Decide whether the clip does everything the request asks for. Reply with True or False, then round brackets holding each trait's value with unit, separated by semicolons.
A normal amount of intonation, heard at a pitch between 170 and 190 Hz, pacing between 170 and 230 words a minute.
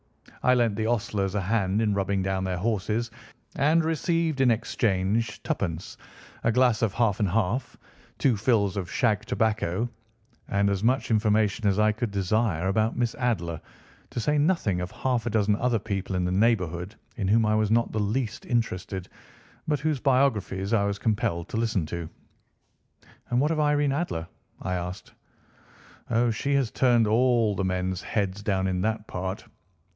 False (3.8 semitones; 110 Hz; 175 wpm)